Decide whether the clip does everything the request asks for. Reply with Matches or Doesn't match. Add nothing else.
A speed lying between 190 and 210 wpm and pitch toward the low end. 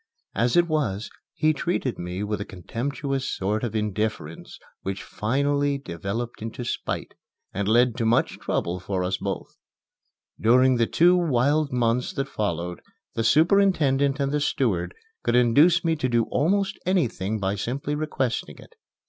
Doesn't match